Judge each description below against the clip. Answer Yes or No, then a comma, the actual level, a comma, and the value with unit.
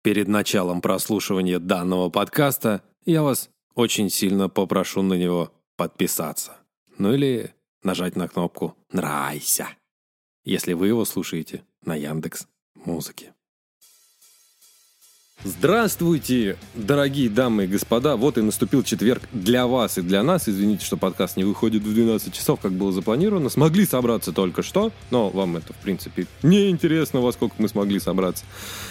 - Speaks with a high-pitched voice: No, low, 105 Hz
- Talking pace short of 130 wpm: No, average, 135 wpm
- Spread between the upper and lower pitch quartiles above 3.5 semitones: Yes, average, 4.9 semitones